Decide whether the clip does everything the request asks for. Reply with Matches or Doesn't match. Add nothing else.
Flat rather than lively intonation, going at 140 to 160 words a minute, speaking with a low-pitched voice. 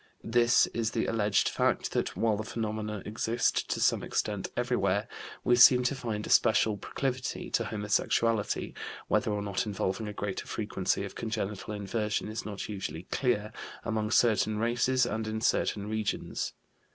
Matches